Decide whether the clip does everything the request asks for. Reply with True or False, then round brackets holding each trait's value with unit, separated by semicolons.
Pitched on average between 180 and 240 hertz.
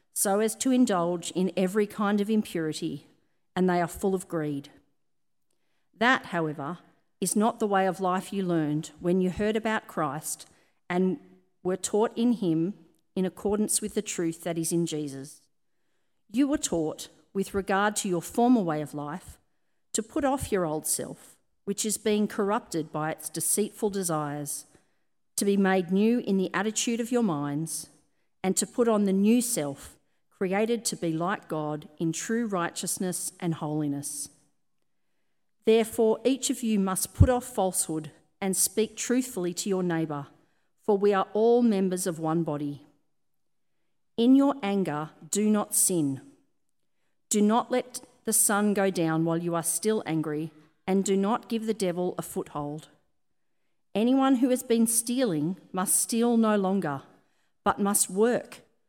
True (190 Hz)